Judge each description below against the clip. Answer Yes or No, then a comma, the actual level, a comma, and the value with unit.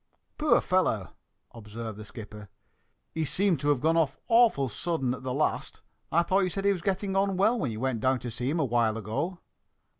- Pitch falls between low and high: Yes, medium, 145 Hz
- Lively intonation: Yes, wide, 8.0 semitones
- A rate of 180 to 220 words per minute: Yes, fast, 205 wpm